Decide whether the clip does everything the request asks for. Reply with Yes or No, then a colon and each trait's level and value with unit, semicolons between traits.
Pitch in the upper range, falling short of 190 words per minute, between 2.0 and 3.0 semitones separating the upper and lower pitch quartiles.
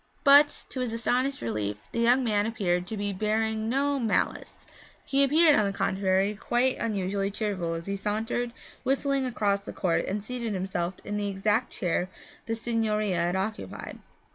No: high, 215 Hz; average, 165 wpm; average, 3.9 semitones